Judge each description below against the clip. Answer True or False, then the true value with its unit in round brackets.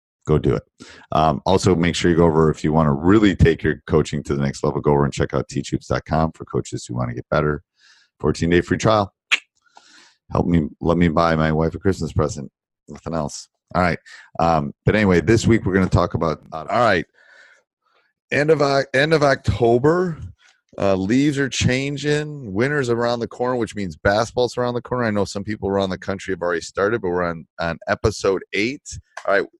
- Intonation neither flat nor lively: False (6.9 semitones)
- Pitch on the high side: False (95 Hz)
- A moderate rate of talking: False (210 wpm)